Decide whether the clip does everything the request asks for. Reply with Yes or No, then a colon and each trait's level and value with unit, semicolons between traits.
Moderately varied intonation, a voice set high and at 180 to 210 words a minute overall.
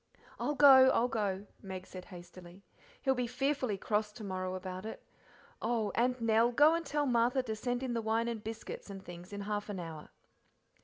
Yes: average, 4.6 semitones; high, 220 Hz; average, 195 wpm